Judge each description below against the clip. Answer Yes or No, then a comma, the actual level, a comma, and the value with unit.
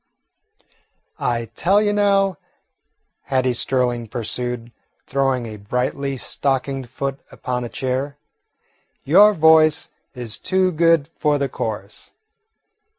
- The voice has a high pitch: No, low, 135 Hz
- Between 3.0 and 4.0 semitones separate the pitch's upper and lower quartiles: No, average, 4.5 semitones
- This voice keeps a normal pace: No, slow, 105 wpm